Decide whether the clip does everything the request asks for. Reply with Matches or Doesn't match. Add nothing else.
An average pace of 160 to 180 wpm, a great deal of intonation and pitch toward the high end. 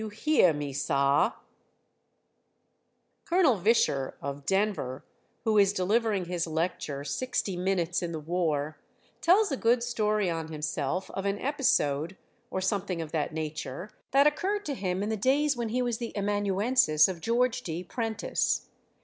Doesn't match